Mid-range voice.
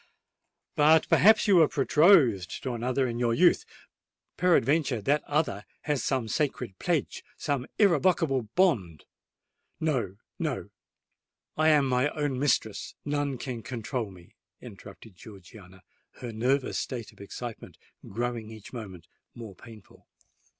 No: low, 125 Hz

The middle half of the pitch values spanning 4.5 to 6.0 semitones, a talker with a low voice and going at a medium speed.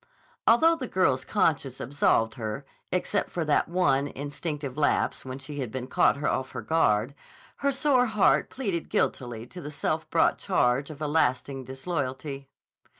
No: average, 5.0 semitones; medium, 145 Hz; average, 155 wpm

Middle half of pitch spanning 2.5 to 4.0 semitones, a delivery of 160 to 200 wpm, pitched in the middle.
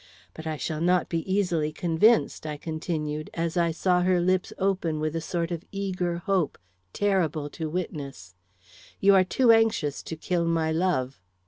Yes: average, 2.9 semitones; average, 165 wpm; medium, 170 Hz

